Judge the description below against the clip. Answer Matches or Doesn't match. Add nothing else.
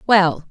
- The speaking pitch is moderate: Doesn't match